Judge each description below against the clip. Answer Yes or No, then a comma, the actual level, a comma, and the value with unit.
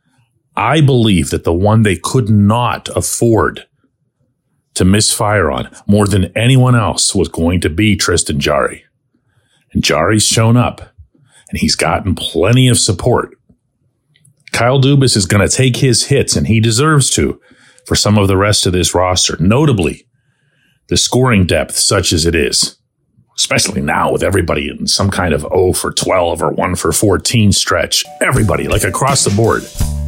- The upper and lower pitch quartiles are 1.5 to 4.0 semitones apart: No, average, 5.1 semitones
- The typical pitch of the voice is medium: No, low, 105 Hz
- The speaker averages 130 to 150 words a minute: No, average, 160 wpm